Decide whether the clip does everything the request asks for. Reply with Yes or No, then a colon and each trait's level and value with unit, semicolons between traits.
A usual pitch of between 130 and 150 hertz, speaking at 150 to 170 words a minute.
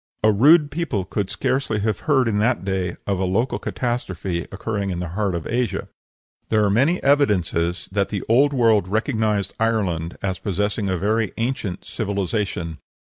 No: low, 105 Hz; average, 165 wpm